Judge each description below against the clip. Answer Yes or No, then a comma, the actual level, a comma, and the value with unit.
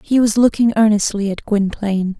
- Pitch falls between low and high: No, high, 210 Hz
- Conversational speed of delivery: Yes, average, 165 wpm